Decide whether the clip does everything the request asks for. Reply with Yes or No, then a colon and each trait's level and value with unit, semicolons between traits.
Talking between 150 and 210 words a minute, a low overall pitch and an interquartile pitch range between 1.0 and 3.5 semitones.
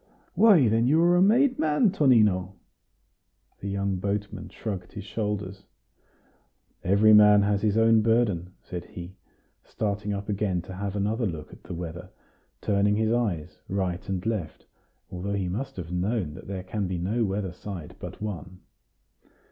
Yes: average, 160 wpm; low, 100 Hz; average, 3.2 semitones